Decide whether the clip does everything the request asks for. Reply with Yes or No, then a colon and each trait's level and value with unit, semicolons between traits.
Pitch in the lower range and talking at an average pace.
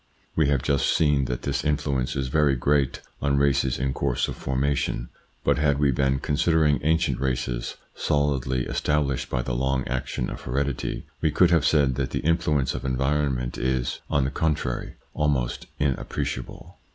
Yes: very low, 70 Hz; average, 165 wpm